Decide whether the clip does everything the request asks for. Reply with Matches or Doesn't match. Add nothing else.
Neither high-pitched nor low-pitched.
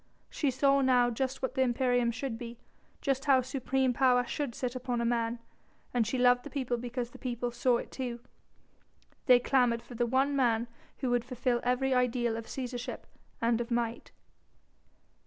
Doesn't match